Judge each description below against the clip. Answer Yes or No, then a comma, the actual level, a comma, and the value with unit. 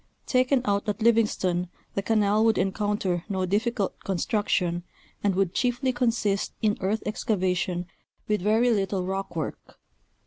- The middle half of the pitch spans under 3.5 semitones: Yes, average, 3.0 semitones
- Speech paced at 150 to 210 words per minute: No, slow, 135 wpm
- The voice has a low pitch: No, high, 205 Hz